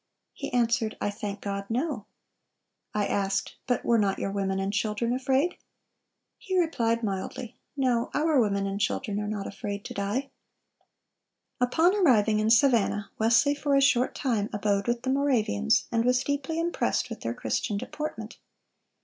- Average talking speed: Yes, average, 160 wpm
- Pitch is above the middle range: Yes, high, 230 Hz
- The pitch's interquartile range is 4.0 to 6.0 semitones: Yes, average, 4.5 semitones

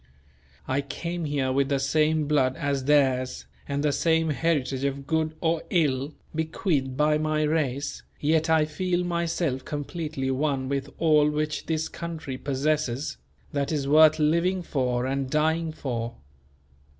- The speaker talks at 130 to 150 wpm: Yes, average, 145 wpm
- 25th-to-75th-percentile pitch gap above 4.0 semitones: No, average, 2.8 semitones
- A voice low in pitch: No, medium, 150 Hz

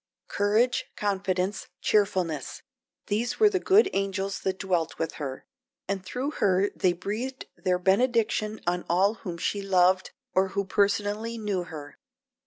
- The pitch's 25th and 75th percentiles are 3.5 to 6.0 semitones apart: No, average, 2.7 semitones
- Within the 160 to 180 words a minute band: No, average, 140 wpm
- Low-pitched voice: No, high, 195 Hz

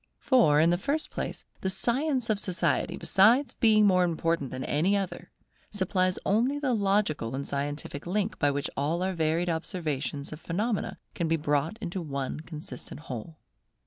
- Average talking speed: Yes, average, 165 wpm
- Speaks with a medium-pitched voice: Yes, medium, 175 Hz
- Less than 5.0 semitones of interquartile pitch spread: No, wide, 5.6 semitones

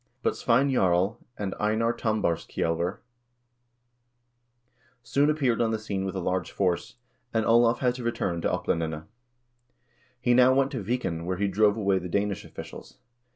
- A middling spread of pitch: Yes, average, 4.6 semitones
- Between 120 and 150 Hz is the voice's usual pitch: No, low, 105 Hz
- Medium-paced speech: Yes, average, 155 wpm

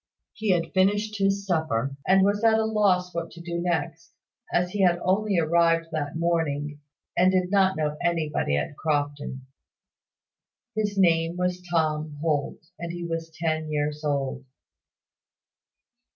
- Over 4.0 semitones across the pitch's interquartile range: No, average, 3.4 semitones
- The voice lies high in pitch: No, medium, 170 Hz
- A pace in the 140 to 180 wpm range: Yes, average, 145 wpm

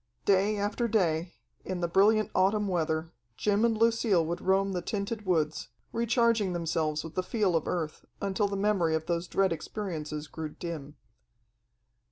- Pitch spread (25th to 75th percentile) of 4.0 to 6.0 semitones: Yes, average, 4.3 semitones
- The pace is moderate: Yes, average, 160 wpm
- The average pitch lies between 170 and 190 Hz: Yes, medium, 185 Hz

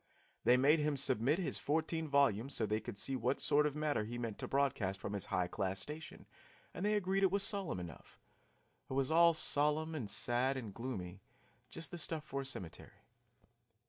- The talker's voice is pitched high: No, low, 135 Hz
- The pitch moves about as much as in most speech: No, wide, 6.2 semitones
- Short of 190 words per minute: No, average, 195 wpm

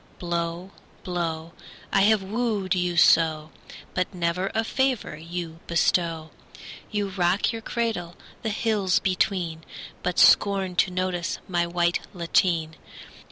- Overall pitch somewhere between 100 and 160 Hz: No, medium, 180 Hz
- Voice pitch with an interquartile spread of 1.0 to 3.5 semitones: Yes, average, 2.7 semitones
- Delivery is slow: Yes, slow, 120 wpm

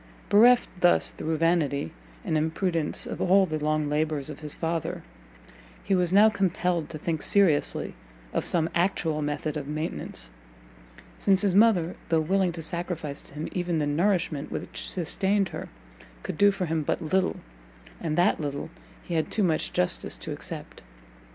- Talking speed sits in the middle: Yes, average, 165 wpm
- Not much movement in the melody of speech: No, average, 3.4 semitones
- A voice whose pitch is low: No, medium, 165 Hz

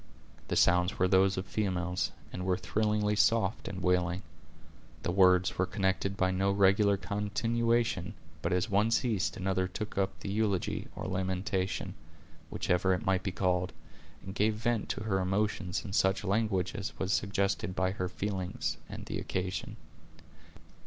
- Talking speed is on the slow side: No, average, 155 wpm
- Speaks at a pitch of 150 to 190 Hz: No, very low, 95 Hz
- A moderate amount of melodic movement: No, narrow, 2.0 semitones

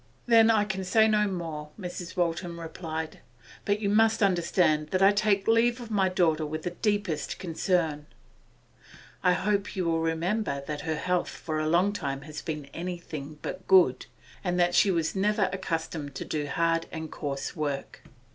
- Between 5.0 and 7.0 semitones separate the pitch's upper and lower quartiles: No, average, 3.9 semitones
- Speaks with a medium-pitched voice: Yes, medium, 175 Hz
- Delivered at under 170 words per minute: No, average, 175 wpm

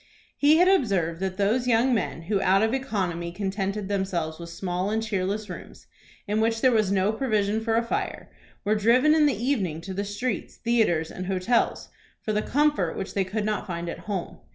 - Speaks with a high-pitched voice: Yes, high, 205 Hz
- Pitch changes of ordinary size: Yes, average, 3.5 semitones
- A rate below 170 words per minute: No, average, 200 wpm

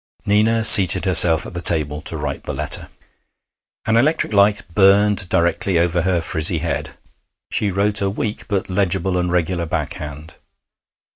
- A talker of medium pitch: No, very low, 90 Hz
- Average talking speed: Yes, average, 155 wpm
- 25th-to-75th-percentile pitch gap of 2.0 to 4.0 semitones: Yes, average, 3.5 semitones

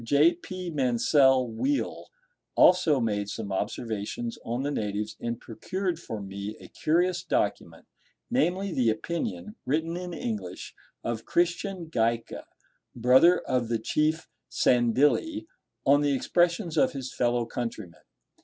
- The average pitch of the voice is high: No, low, 130 Hz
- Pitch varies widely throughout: Yes, wide, 6.9 semitones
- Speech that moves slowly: Yes, slow, 125 wpm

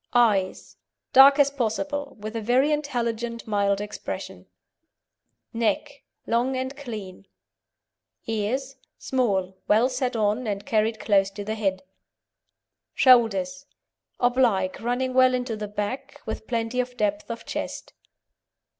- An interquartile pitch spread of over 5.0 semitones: No, average, 3.7 semitones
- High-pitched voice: Yes, high, 230 Hz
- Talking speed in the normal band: No, slow, 120 wpm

